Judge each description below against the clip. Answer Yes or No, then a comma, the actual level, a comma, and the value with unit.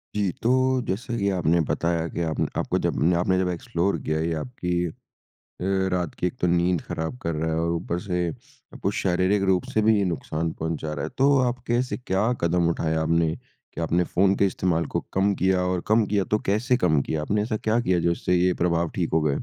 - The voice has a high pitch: No, very low, 90 Hz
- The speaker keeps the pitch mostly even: No, average, 3.1 semitones